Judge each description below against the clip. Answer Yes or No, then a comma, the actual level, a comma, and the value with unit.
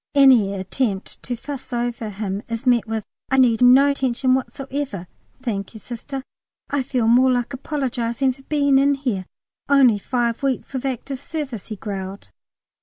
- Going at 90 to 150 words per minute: No, average, 160 wpm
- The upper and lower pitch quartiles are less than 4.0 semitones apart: Yes, average, 3.4 semitones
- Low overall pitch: No, very high, 250 Hz